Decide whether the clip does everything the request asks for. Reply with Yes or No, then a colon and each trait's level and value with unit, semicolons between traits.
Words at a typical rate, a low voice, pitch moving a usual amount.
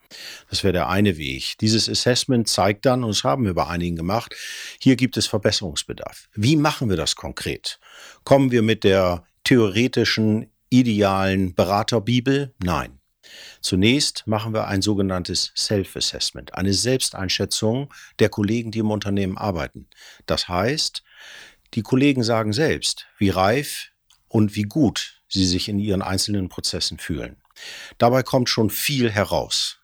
Yes: average, 140 wpm; low, 105 Hz; average, 3.8 semitones